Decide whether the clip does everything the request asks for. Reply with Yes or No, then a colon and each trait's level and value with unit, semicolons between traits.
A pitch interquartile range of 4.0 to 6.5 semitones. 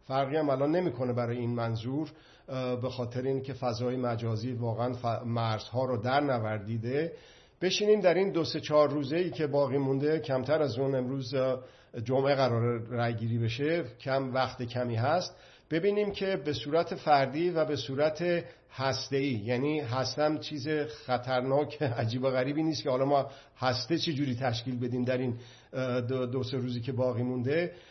No: average, 3.3 semitones